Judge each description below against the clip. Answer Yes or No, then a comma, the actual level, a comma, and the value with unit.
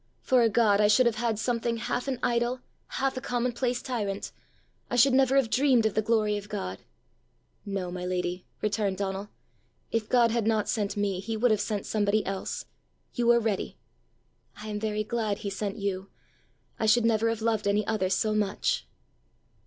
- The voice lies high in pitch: Yes, high, 215 Hz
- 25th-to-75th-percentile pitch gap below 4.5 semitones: Yes, average, 2.8 semitones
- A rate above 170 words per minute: Yes, average, 185 wpm